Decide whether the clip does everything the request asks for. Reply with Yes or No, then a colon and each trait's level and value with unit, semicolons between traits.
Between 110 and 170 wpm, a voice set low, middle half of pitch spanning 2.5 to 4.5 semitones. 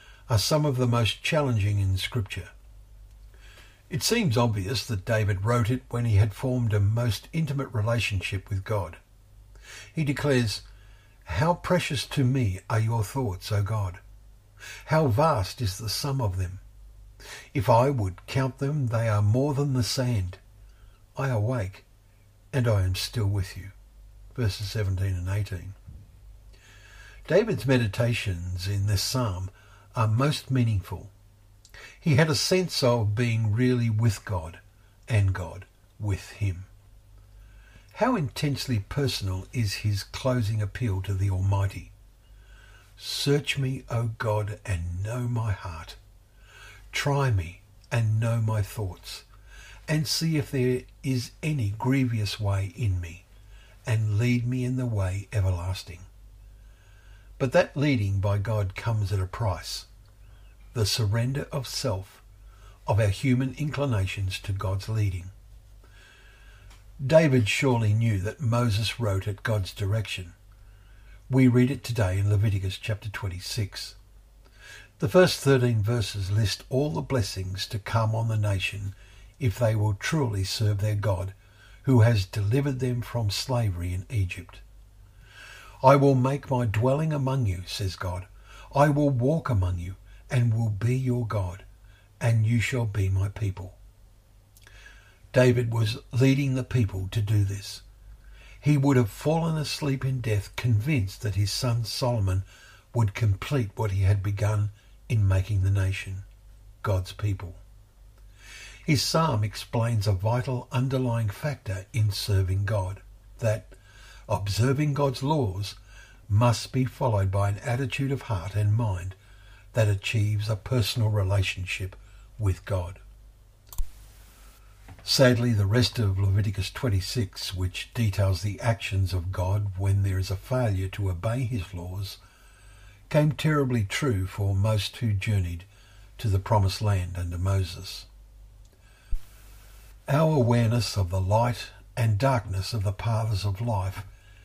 Yes: slow, 135 wpm; low, 105 Hz; average, 3.3 semitones